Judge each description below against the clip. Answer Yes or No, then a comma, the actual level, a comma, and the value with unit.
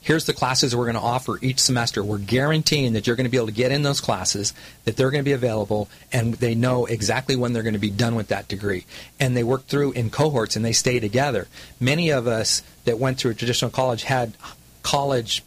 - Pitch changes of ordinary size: Yes, average, 3.0 semitones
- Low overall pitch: Yes, low, 125 Hz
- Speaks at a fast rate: Yes, fast, 240 wpm